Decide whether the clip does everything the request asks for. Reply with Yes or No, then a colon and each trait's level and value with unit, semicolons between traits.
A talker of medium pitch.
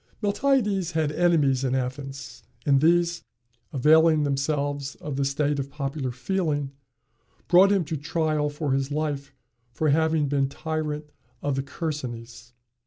Yes: medium, 145 Hz